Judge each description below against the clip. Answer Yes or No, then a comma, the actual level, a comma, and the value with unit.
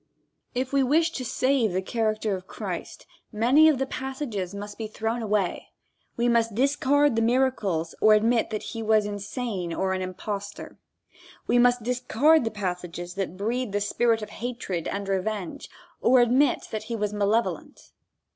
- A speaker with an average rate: Yes, average, 165 wpm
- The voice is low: No, high, 220 Hz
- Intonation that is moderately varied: Yes, average, 3.6 semitones